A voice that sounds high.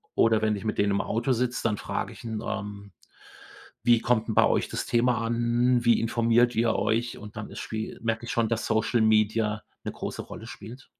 No: low, 115 Hz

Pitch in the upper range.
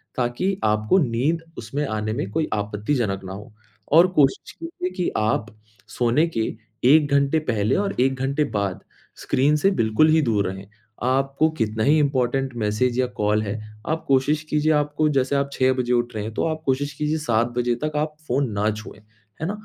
No: low, 130 Hz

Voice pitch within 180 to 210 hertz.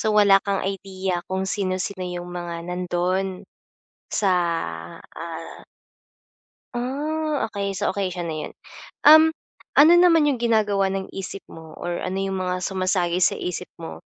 Yes: high, 190 Hz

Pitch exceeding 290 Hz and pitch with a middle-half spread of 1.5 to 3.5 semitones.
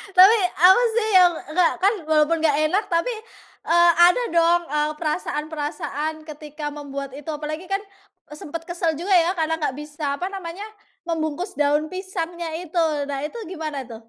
Yes: very high, 320 Hz; average, 2.9 semitones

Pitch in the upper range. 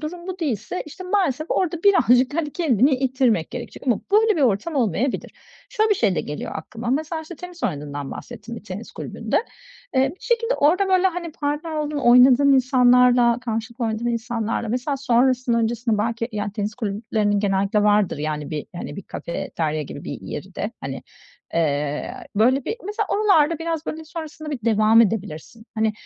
Yes: high, 245 Hz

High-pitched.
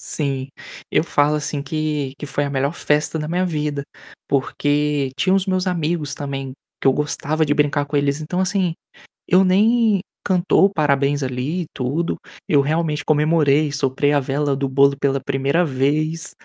No: medium, 150 Hz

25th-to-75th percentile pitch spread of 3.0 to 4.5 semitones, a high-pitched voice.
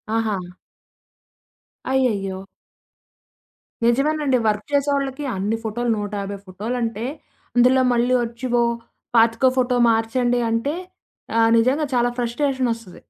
No: narrow, 2.5 semitones; high, 235 Hz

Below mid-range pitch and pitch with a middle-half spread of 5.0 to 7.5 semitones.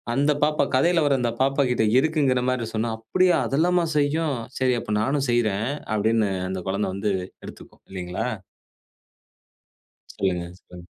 Yes: low, 125 Hz; average, 5.3 semitones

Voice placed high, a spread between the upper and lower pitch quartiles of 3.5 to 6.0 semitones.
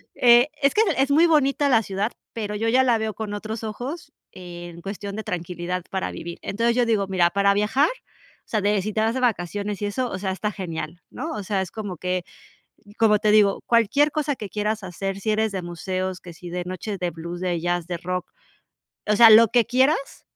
Yes: high, 205 Hz; average, 4.0 semitones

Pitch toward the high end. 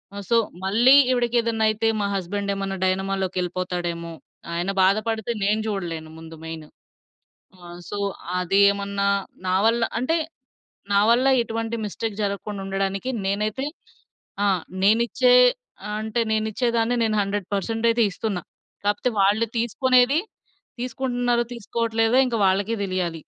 Yes: high, 210 Hz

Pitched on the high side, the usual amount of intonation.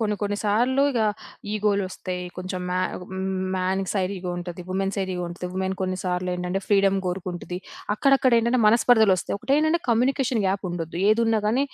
Yes: high, 195 Hz; average, 3.7 semitones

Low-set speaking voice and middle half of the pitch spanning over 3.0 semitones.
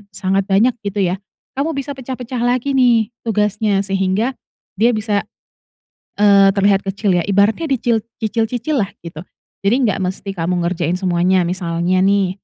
No: high, 200 Hz; average, 3.6 semitones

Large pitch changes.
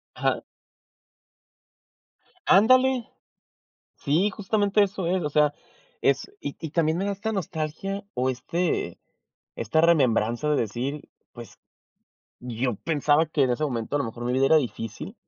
Yes: wide, 7.1 semitones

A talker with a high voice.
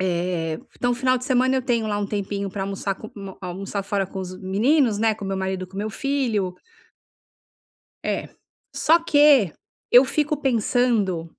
Yes: high, 205 Hz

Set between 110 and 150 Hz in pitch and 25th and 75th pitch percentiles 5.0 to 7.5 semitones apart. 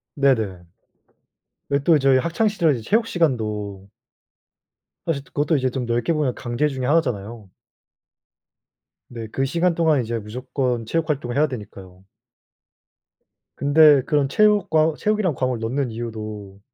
Yes: low, 135 Hz; wide, 5.4 semitones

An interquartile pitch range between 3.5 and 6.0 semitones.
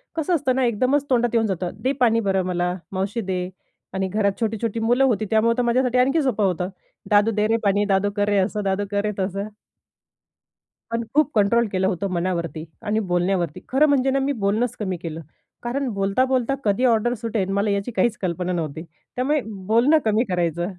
Yes: average, 4.3 semitones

